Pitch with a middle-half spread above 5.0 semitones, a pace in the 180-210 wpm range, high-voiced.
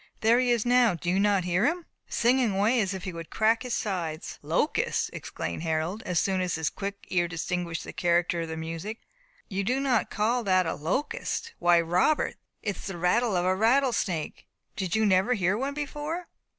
Yes: wide, 5.5 semitones; fast, 205 wpm; high, 195 Hz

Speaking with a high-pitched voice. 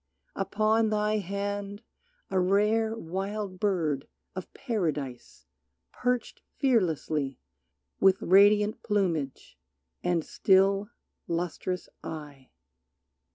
Yes: high, 195 Hz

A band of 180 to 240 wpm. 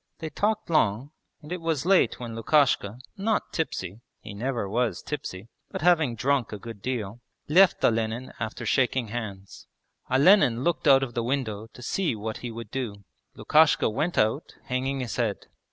No: average, 170 wpm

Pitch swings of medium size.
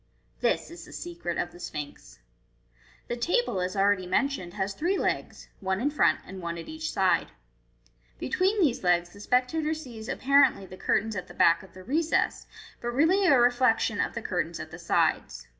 No: wide, 8.5 semitones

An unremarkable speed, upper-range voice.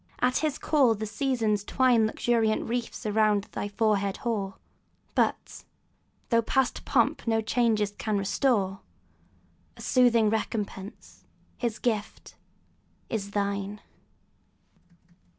No: slow, 105 wpm; high, 220 Hz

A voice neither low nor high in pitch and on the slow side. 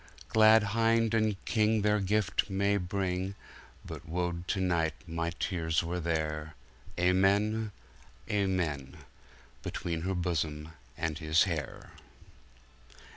No: very low, 90 Hz; slow, 90 wpm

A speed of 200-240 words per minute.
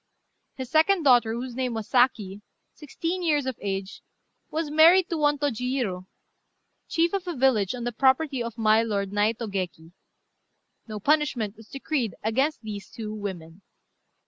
No: average, 150 wpm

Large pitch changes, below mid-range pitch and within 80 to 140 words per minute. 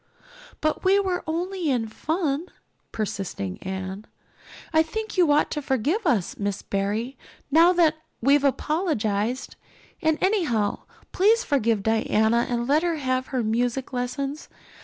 No: wide, 6.5 semitones; very high, 270 Hz; slow, 135 wpm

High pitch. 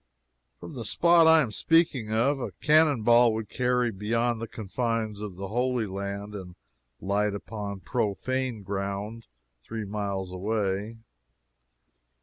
No: low, 110 Hz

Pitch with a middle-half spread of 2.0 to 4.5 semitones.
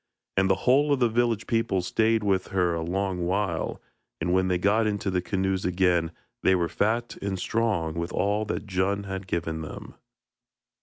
Yes: average, 3.1 semitones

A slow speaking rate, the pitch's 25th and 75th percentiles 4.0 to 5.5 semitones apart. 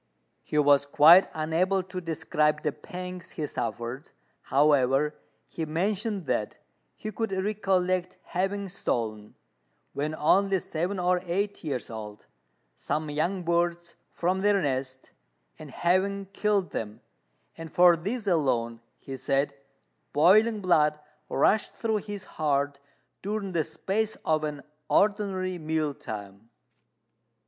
Yes: slow, 120 wpm; average, 4.9 semitones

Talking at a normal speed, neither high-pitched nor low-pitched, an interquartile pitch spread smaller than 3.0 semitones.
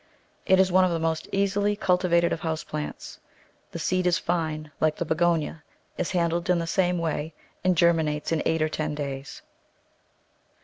Yes: average, 175 wpm; medium, 170 Hz; narrow, 2.4 semitones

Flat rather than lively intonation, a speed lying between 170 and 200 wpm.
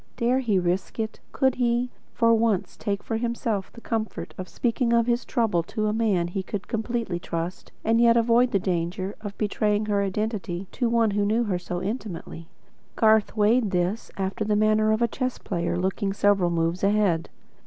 No: average, 3.6 semitones; average, 185 wpm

